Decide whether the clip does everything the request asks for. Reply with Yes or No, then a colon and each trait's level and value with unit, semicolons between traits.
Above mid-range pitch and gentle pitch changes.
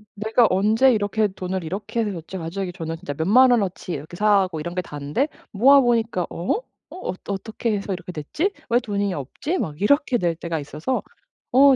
No: high, 200 Hz; average, 5.3 semitones